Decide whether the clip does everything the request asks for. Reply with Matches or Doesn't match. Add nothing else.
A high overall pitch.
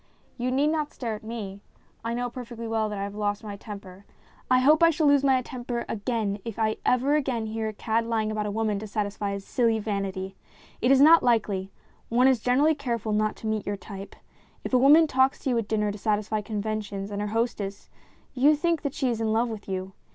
Matches